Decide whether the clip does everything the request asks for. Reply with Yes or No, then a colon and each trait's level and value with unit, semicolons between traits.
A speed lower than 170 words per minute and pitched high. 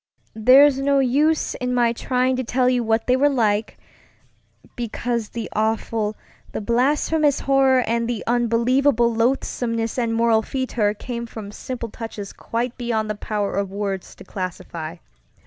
Yes: average, 145 wpm; high, 235 Hz